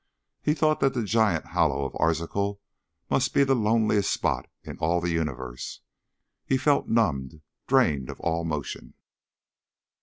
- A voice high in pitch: No, very low, 85 Hz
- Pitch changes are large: Yes, wide, 7.1 semitones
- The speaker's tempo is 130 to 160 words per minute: Yes, average, 145 wpm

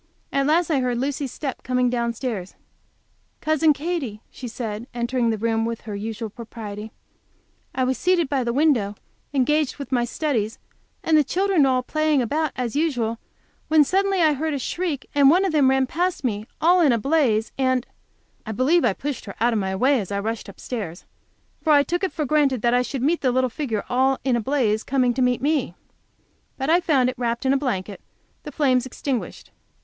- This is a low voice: No, very high, 260 Hz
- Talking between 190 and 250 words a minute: Yes, average, 200 wpm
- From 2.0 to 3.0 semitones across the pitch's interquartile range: No, average, 4.3 semitones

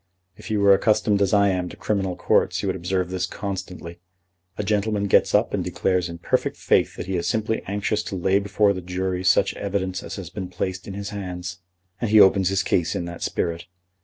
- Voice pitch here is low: Yes, very low, 95 Hz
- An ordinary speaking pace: No, fast, 220 wpm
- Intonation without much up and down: Yes, narrow, 2.0 semitones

